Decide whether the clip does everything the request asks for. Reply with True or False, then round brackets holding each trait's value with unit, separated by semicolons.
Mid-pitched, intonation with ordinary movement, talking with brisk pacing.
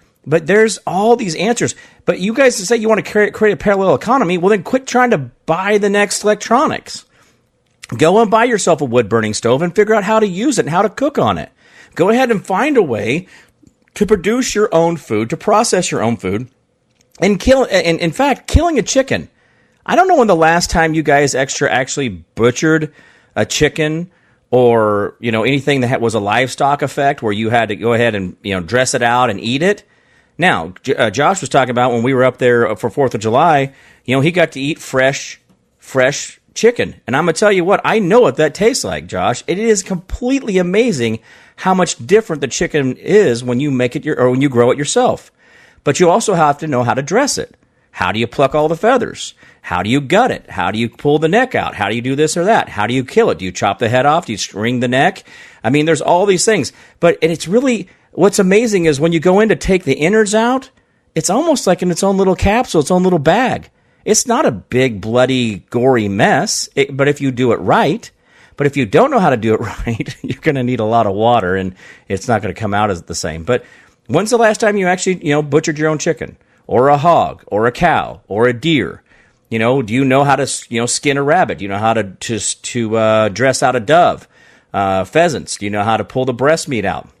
False (150 Hz; 8.8 semitones; 245 wpm)